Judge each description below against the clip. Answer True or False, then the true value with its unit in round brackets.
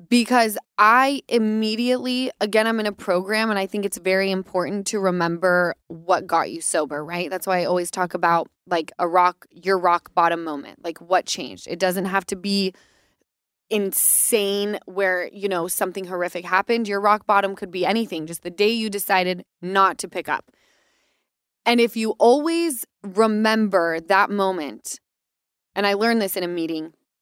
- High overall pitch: True (195 Hz)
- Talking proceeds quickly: False (170 wpm)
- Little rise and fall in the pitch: False (3.2 semitones)